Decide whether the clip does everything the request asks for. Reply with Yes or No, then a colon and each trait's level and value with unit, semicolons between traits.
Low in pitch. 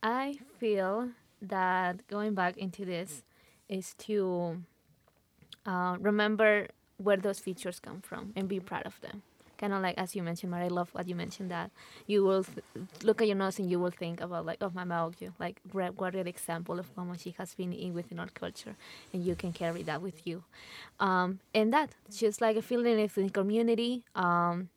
No: high, 190 Hz